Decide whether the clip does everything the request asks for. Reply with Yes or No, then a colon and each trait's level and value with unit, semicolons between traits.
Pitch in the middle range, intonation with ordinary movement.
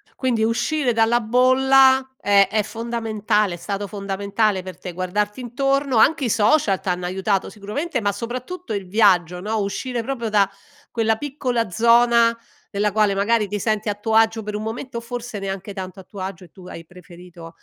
No: high, 215 Hz; average, 3.2 semitones